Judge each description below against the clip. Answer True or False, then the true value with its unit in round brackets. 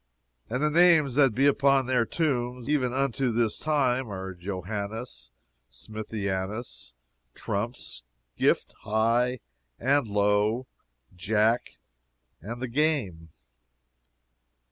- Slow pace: True (100 wpm)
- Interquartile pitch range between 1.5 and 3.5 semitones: False (4.5 semitones)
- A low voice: True (120 Hz)